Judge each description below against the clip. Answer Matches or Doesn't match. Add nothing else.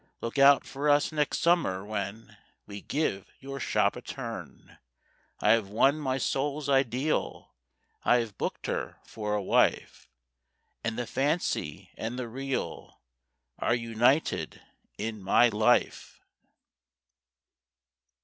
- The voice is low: Matches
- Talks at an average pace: Doesn't match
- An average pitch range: Matches